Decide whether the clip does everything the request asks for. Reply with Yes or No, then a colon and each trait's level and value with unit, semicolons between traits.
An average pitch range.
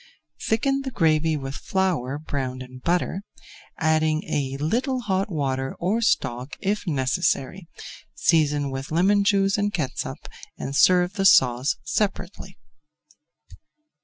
No: wide, 6.3 semitones